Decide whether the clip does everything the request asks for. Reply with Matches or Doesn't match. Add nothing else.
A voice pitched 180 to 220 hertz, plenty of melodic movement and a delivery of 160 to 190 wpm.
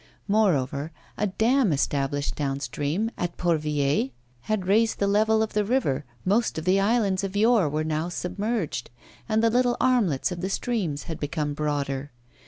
Matches